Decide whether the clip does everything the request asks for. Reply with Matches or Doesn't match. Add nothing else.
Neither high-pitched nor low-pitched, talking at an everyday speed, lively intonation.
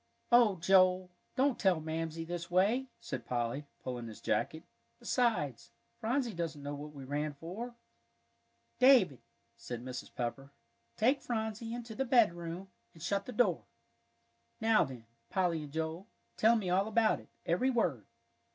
Matches